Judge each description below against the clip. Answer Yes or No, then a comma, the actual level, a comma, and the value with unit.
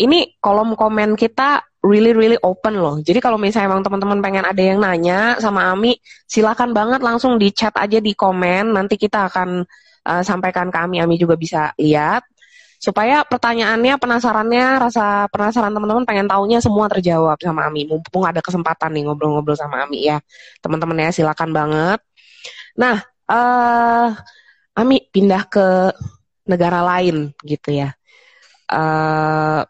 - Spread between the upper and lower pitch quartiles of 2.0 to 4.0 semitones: No, average, 5.2 semitones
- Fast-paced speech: Yes, fast, 145 wpm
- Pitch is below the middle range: No, high, 195 Hz